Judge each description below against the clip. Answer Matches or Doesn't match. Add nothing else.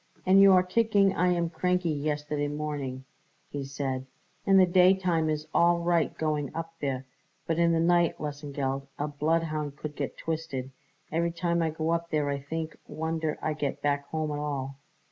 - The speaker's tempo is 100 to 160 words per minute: Doesn't match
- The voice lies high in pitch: Doesn't match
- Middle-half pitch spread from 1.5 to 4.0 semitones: Matches